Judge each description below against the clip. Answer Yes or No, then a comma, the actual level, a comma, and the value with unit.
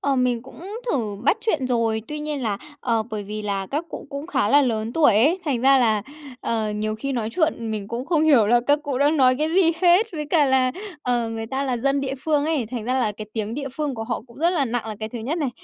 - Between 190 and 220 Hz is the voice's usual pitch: No, very high, 255 Hz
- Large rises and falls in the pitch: No, average, 4.7 semitones